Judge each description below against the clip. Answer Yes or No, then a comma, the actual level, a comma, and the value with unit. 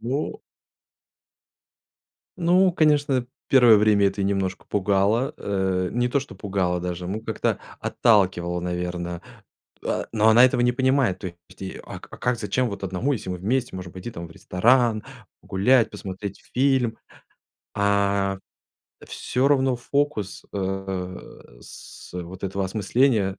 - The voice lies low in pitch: Yes, low, 100 Hz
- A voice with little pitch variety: No, average, 4.8 semitones